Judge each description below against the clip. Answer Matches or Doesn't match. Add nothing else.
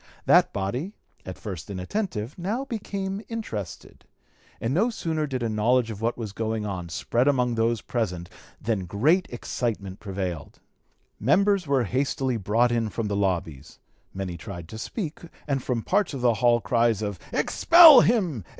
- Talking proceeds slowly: Doesn't match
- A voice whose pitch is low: Matches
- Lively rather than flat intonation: Matches